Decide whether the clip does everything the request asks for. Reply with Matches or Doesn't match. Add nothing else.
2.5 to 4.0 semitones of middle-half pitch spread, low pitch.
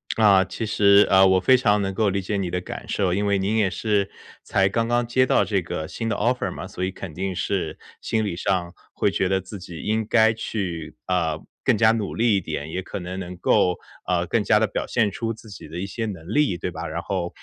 Matches